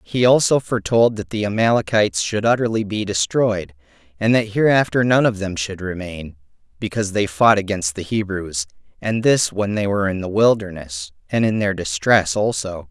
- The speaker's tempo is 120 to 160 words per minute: No, average, 170 wpm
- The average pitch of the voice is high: No, low, 100 Hz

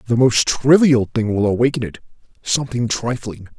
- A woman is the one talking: No, male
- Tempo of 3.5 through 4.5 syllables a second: No, 5.2 syllables/s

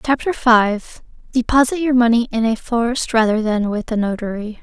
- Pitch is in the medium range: No, high, 230 Hz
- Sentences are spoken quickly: No, average, 155 wpm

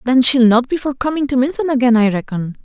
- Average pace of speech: No, fast, 250 wpm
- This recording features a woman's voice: Yes, female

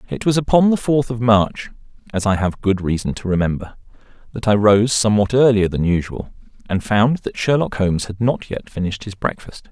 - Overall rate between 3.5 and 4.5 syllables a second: No, 5.5 syllables/s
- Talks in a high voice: No, low, 110 Hz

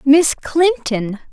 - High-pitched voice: Yes, very high, 275 Hz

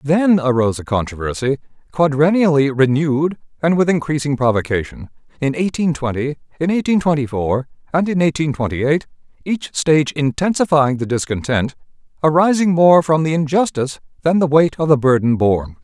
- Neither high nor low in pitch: Yes, medium, 150 Hz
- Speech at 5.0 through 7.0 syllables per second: Yes, 5.5 syllables/s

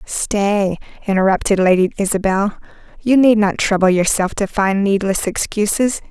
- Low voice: No, high, 200 Hz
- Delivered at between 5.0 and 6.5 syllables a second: No, 4.6 syllables/s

